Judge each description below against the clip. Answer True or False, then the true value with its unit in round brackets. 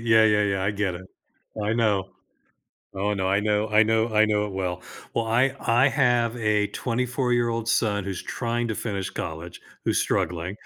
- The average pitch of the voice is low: True (105 Hz)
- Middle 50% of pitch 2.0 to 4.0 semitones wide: True (2.9 semitones)